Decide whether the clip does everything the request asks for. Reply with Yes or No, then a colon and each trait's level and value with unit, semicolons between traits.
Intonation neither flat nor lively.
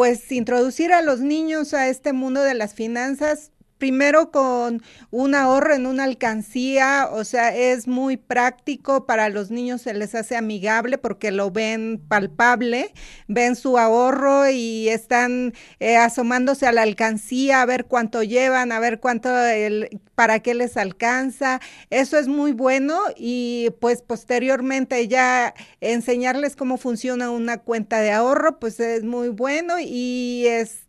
No: narrow, 2.3 semitones